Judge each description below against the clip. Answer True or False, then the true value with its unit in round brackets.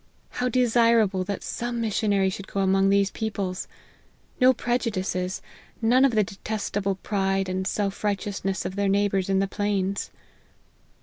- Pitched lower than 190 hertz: False (200 Hz)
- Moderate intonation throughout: False (2.3 semitones)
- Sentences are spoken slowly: False (145 wpm)